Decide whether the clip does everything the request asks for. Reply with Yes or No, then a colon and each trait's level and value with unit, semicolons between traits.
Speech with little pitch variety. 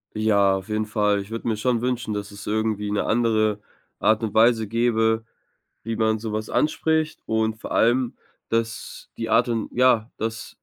Yes: narrow, 1.4 semitones